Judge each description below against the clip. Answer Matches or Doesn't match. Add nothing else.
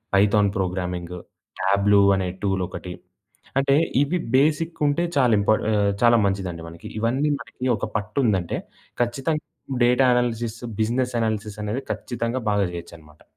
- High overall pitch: Doesn't match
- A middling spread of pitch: Matches